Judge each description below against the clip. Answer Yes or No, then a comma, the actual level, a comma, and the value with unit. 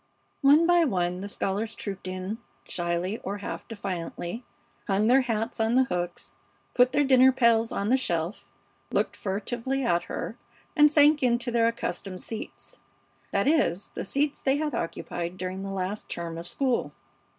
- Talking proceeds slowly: No, average, 160 wpm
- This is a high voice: Yes, high, 220 Hz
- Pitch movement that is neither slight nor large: No, wide, 5.9 semitones